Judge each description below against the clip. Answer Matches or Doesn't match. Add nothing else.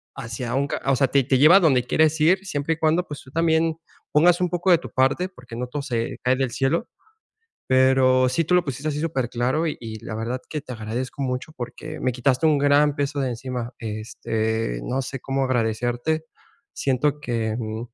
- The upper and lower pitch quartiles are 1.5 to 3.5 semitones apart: Doesn't match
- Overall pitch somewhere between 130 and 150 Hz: Matches